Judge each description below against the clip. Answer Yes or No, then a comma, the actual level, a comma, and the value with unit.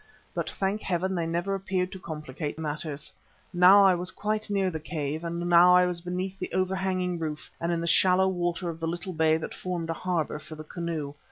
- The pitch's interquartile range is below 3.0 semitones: Yes, narrow, 2.4 semitones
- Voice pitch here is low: No, medium, 175 Hz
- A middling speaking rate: No, fast, 210 wpm